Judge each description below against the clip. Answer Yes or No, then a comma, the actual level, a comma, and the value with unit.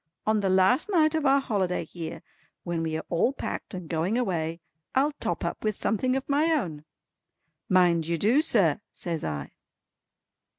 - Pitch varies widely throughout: Yes, wide, 8.1 semitones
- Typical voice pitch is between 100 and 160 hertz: No, high, 190 Hz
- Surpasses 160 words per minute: Yes, average, 170 wpm